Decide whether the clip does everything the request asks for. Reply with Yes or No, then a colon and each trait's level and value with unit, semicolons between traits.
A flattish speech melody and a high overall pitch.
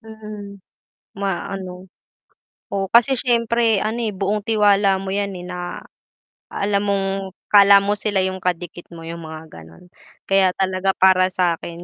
Yes: narrow, 2.3 semitones; high, 195 Hz